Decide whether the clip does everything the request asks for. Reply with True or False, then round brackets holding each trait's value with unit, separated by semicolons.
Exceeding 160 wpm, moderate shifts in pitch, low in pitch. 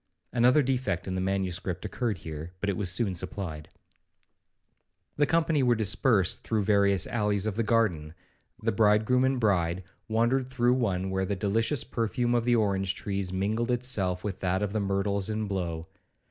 True (170 wpm; 3.9 semitones; 105 Hz)